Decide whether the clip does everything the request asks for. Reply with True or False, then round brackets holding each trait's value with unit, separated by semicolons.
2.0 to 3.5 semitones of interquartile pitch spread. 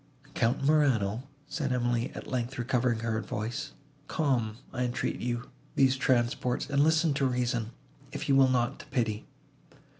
True (2.5 semitones)